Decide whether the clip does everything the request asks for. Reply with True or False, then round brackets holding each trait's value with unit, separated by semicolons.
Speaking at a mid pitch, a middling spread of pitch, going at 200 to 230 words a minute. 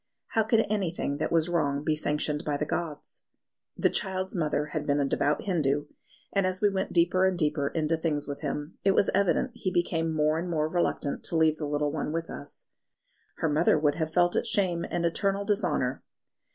True (160 Hz; 3.8 semitones; 205 wpm)